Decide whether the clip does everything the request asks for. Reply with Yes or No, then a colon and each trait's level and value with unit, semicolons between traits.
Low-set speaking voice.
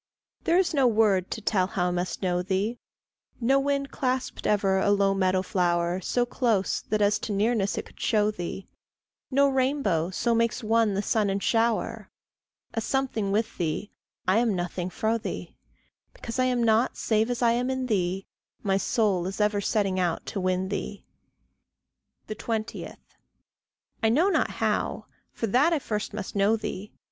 No: high, 210 Hz